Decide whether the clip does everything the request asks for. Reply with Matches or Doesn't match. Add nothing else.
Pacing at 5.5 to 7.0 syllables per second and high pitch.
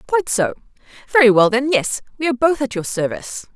Matches